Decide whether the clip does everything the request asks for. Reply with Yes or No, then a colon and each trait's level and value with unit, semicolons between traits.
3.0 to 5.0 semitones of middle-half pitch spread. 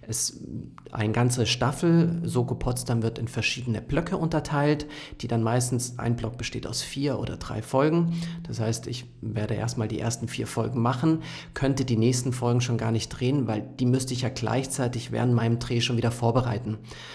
No: narrow, 2.6 semitones